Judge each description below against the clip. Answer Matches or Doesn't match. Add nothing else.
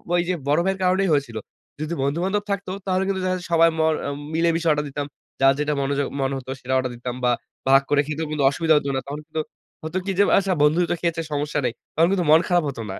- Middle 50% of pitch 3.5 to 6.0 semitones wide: Matches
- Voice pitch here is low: Doesn't match